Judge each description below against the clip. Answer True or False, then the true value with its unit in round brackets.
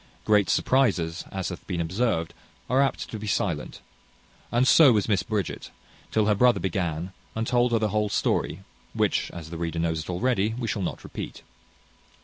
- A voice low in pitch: True (100 Hz)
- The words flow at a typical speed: True (180 wpm)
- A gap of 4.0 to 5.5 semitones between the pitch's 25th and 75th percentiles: True (4.9 semitones)